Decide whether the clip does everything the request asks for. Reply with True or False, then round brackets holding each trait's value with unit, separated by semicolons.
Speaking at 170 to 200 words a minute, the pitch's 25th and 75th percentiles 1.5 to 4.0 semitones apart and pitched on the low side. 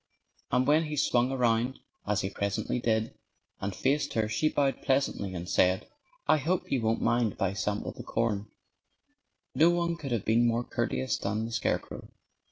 False (175 wpm; 4.5 semitones; 115 Hz)